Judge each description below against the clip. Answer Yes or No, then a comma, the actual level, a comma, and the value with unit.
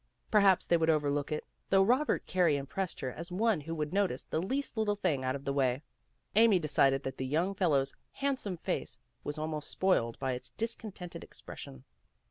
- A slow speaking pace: No, average, 185 wpm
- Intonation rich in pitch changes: Yes, wide, 5.8 semitones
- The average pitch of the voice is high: No, medium, 165 Hz